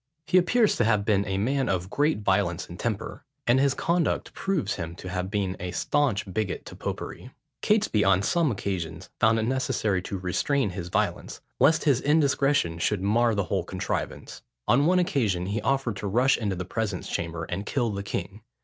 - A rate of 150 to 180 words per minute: No, average, 190 wpm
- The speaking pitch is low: Yes, low, 105 Hz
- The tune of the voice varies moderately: No, wide, 6.3 semitones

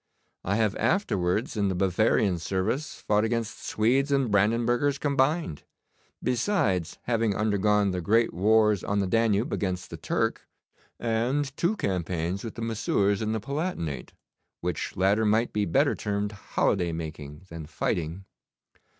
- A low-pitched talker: Yes, low, 105 Hz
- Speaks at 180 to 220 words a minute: No, average, 140 wpm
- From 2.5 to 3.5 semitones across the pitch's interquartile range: No, average, 3.9 semitones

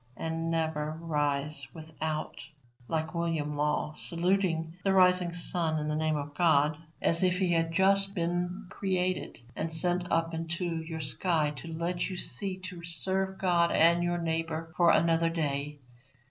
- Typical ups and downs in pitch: No, narrow, 2.1 semitones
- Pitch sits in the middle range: Yes, medium, 165 Hz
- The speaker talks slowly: No, average, 155 wpm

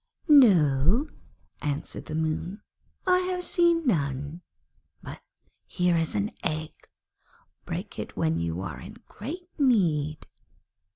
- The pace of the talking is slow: Yes, slow, 115 wpm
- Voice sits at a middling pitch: Yes, medium, 165 Hz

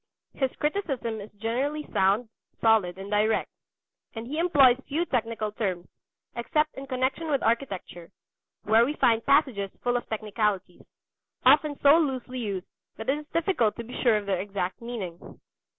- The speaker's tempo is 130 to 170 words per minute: Yes, average, 155 wpm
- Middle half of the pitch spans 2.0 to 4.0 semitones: No, average, 5.0 semitones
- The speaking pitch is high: Yes, high, 235 Hz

